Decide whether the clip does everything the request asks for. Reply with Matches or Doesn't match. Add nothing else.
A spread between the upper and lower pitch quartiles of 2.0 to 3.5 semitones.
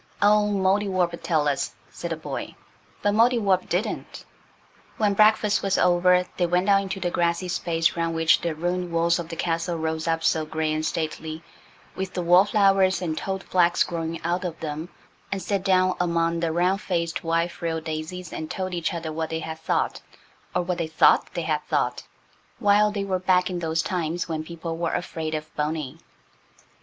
Matches